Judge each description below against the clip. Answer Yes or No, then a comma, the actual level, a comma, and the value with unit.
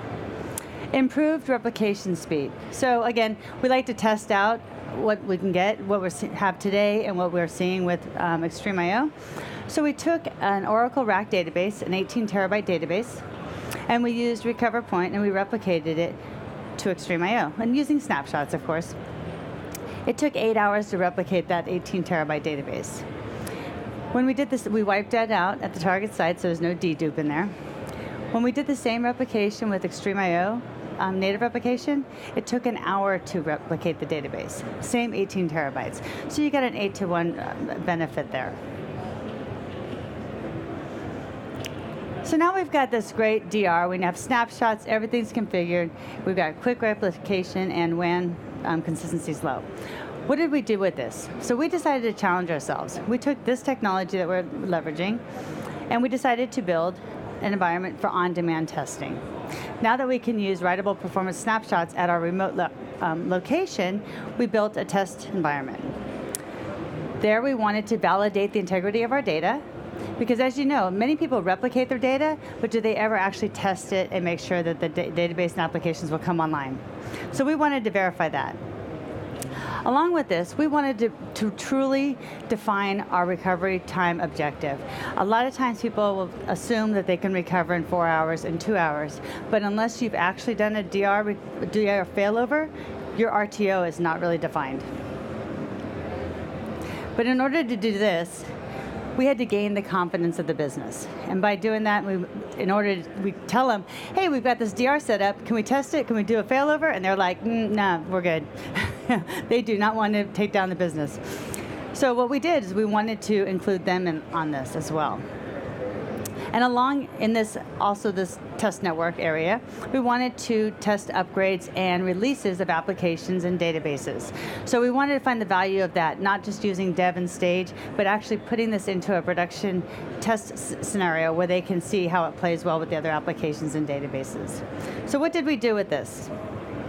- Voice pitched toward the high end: Yes, high, 200 Hz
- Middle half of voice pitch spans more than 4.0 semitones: Yes, average, 4.9 semitones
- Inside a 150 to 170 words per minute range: No, average, 180 wpm